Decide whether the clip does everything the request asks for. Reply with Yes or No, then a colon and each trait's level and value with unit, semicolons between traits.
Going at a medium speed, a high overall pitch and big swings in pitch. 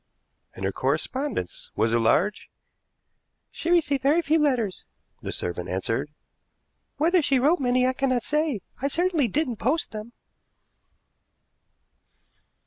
No: slow, 125 wpm; very high, 255 Hz; wide, 8.6 semitones